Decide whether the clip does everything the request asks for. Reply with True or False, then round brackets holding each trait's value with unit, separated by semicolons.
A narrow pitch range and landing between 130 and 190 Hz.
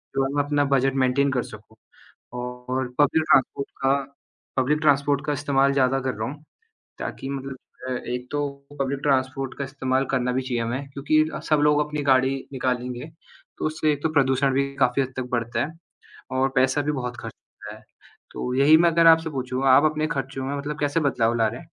True (2.1 semitones; 135 Hz)